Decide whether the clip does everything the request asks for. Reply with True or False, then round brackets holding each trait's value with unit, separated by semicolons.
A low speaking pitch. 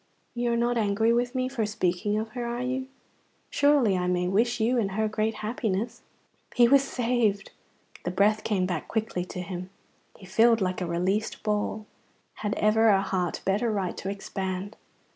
False (215 Hz)